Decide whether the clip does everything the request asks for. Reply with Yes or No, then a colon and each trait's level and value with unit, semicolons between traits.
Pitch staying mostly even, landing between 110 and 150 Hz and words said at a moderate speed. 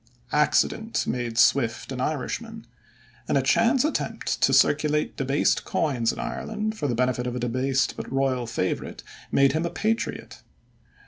No: average, 4.6 semitones; low, 135 Hz; average, 150 wpm